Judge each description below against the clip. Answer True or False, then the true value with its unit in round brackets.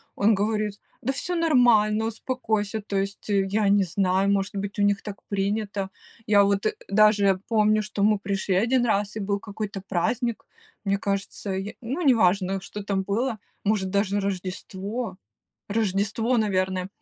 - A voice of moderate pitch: False (205 Hz)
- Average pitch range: False (1.8 semitones)